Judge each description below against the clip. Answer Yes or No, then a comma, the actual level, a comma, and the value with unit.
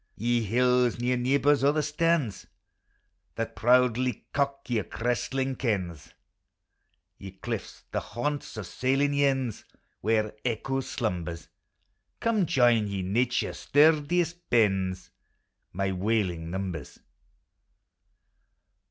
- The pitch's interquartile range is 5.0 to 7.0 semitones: Yes, wide, 5.5 semitones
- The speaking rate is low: Yes, slow, 100 wpm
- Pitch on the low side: Yes, low, 120 Hz